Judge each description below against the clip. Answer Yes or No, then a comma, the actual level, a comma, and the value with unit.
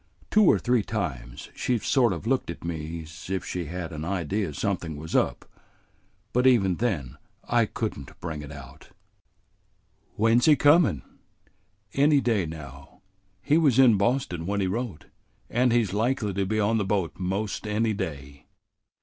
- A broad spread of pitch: Yes, wide, 6.5 semitones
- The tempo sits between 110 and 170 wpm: Yes, average, 165 wpm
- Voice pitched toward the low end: Yes, low, 100 Hz